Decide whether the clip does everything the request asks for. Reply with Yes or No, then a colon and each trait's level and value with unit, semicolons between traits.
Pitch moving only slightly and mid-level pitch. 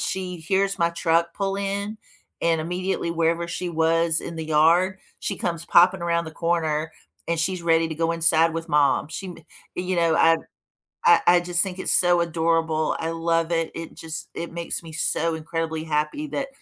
Yes: narrow, 1.5 semitones; medium, 170 Hz